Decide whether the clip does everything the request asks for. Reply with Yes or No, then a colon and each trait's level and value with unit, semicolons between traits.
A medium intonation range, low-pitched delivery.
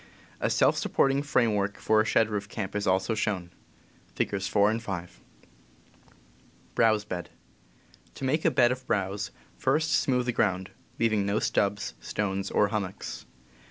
Yes: average, 3.1 semitones; low, 105 Hz